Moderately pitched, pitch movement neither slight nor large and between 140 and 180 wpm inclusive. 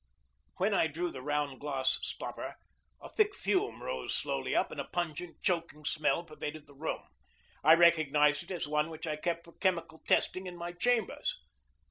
Yes: medium, 165 Hz; average, 3.0 semitones; average, 175 wpm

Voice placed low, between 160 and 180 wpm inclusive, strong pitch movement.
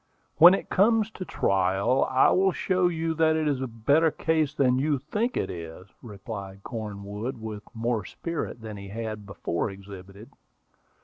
Yes: low, 120 Hz; average, 165 wpm; wide, 8.0 semitones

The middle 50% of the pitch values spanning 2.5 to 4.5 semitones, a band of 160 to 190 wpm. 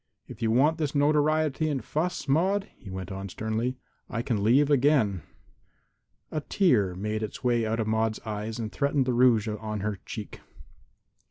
No: average, 5.2 semitones; average, 170 wpm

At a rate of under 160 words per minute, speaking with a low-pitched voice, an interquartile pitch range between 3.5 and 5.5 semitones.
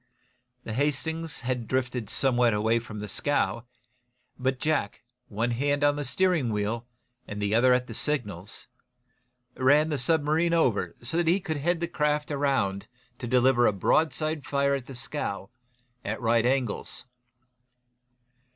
Yes: average, 145 wpm; low, 130 Hz; average, 4.4 semitones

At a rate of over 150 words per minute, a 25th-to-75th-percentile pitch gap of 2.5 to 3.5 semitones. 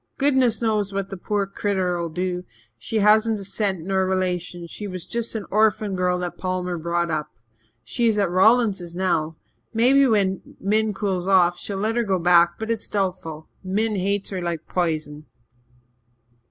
Yes: average, 170 wpm; average, 3.2 semitones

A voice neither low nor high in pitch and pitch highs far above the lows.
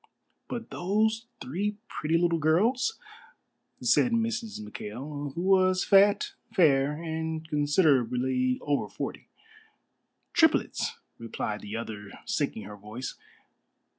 Yes: medium, 160 Hz; wide, 7.9 semitones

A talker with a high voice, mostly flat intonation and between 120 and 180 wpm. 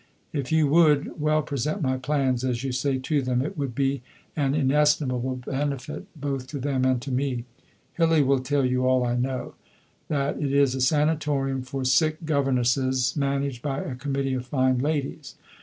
No: low, 135 Hz; narrow, 2.2 semitones; average, 175 wpm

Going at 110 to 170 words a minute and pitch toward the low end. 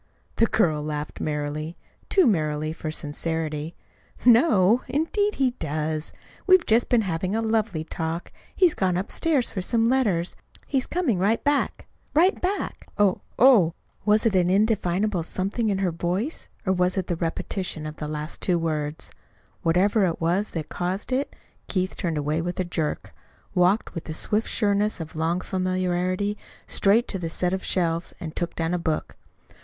No: average, 165 wpm; medium, 185 Hz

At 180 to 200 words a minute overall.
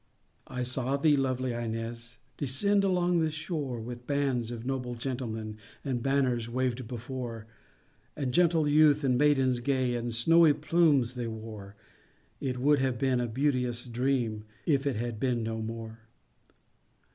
No: average, 145 wpm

